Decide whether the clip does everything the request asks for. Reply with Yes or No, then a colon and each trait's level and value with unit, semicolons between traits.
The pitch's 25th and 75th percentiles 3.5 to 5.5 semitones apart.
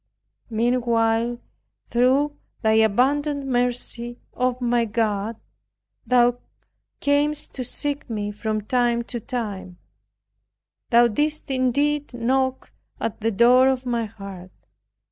No: narrow, 2.6 semitones